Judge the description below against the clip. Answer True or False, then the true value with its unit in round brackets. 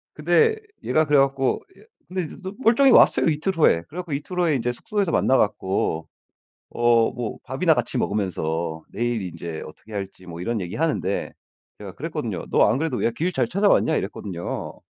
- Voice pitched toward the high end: False (125 Hz)